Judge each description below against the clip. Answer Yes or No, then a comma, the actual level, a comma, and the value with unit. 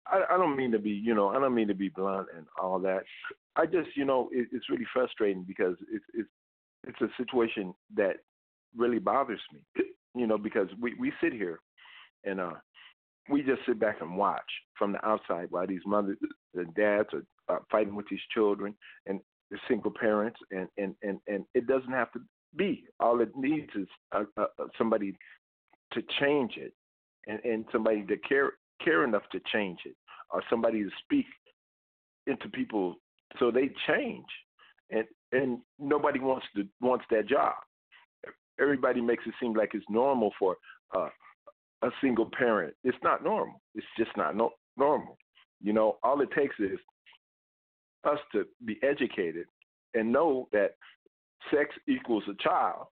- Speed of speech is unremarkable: Yes, average, 170 wpm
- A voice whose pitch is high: No, low, 120 Hz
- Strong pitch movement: Yes, wide, 6.3 semitones